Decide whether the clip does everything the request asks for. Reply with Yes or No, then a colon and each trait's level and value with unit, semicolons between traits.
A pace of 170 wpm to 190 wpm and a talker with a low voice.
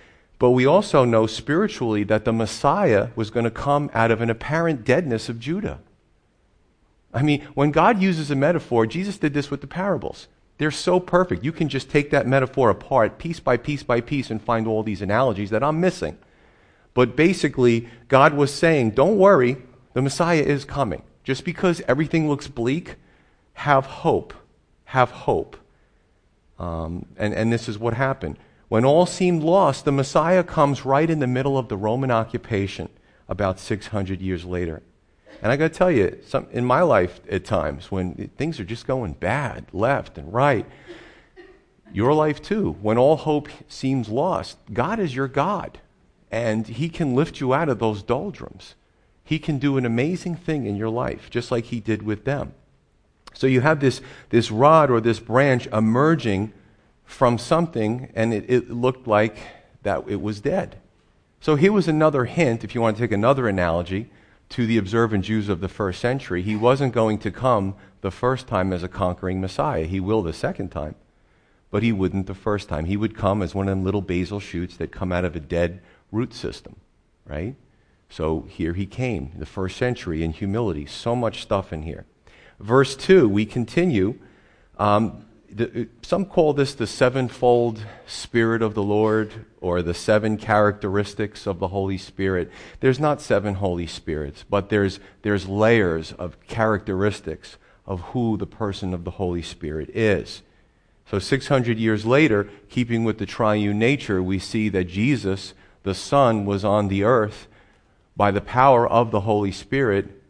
Yes: average, 175 wpm; low, 115 Hz